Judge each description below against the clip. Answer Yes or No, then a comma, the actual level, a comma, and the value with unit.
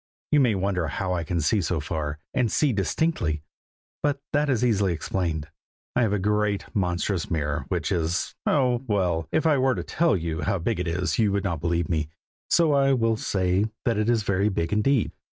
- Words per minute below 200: No, fast, 205 wpm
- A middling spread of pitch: No, wide, 5.7 semitones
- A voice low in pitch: Yes, low, 100 Hz